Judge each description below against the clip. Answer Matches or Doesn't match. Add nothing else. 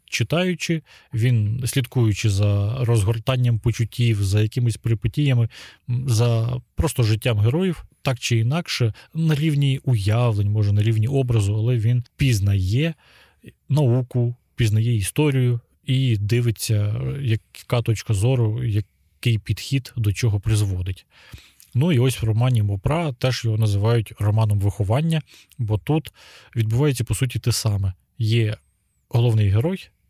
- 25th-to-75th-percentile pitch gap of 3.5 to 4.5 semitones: Doesn't match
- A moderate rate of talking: Matches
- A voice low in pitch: Matches